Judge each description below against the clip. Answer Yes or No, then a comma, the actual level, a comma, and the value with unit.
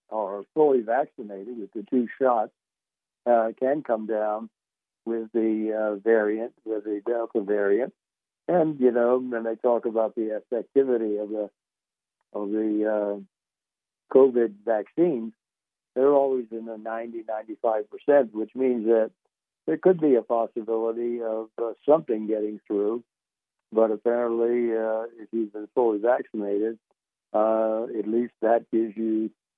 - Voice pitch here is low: Yes, low, 115 Hz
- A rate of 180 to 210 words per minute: No, average, 140 wpm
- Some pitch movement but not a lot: No, narrow, 1.7 semitones